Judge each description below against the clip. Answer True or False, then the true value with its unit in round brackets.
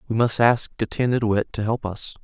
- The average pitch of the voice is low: True (115 Hz)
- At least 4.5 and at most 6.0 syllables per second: True (5.8 syllables/s)